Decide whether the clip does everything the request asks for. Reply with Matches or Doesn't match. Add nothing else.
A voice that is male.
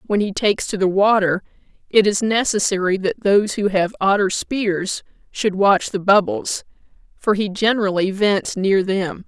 Doesn't match